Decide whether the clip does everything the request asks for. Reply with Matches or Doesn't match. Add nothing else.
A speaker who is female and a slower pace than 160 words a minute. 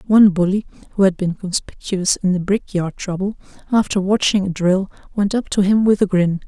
Doesn't match